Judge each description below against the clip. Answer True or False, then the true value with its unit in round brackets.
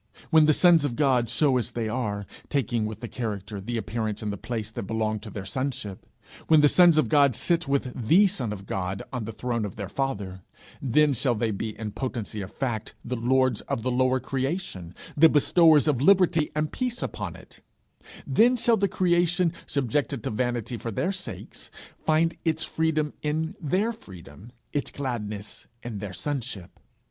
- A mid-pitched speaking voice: False (125 Hz)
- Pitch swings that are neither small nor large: False (6.1 semitones)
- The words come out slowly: False (185 wpm)